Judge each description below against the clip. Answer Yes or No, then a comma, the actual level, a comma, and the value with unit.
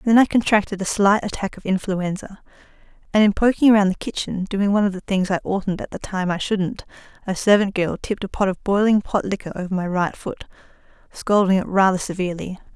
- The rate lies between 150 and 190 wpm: No, fast, 205 wpm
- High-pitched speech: Yes, high, 195 Hz